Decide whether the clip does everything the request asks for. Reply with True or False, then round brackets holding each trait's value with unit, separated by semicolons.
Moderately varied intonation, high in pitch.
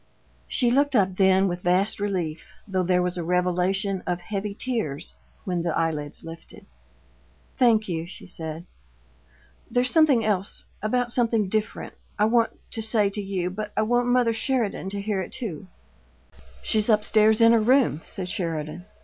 True (4.0 semitones; 200 Hz)